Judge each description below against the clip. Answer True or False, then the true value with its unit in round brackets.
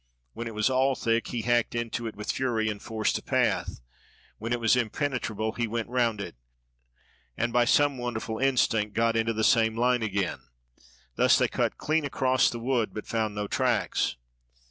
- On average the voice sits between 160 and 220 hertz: False (115 Hz)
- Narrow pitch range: True (2.0 semitones)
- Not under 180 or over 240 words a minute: True (185 wpm)